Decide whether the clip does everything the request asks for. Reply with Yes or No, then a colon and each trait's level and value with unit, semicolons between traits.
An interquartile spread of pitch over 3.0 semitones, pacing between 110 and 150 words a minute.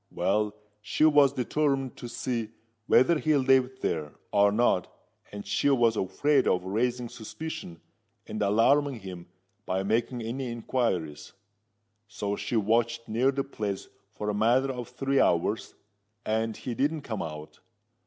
Yes: average, 4.5 semitones; average, 140 wpm